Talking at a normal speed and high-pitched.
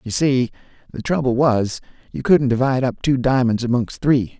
No: average, 175 wpm; low, 130 Hz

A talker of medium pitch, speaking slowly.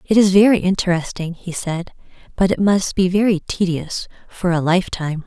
No: medium, 180 Hz; average, 170 wpm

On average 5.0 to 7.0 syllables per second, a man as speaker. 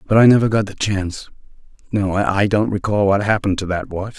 Yes: 5.8 syllables/s; male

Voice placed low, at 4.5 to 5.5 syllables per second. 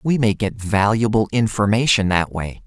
Yes: low, 105 Hz; 4.7 syllables/s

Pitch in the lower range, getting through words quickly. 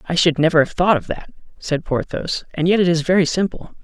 No: medium, 170 Hz; fast, 235 wpm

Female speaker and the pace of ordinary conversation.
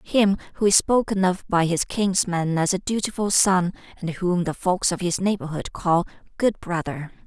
Yes: female; average, 180 wpm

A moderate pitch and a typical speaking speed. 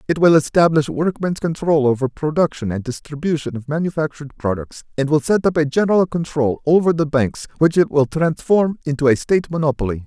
Yes: medium, 150 Hz; average, 180 wpm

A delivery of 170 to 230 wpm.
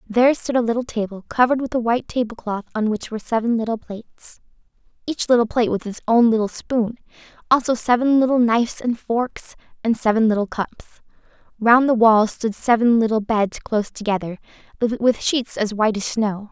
Yes: average, 175 wpm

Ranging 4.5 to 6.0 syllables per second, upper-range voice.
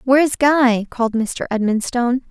Yes: 4.9 syllables/s; high, 245 Hz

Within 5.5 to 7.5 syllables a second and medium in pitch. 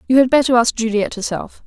No: 6.1 syllables/s; high, 240 Hz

